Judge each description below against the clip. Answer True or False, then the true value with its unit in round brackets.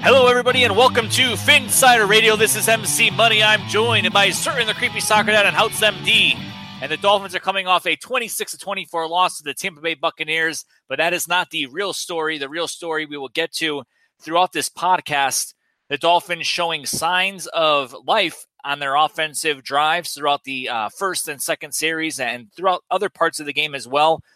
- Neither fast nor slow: True (195 wpm)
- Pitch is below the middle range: False (165 Hz)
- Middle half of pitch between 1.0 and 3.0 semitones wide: False (4.8 semitones)